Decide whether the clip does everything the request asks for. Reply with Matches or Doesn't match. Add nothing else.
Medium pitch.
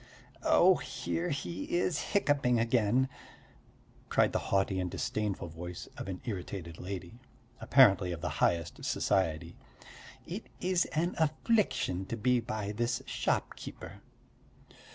Doesn't match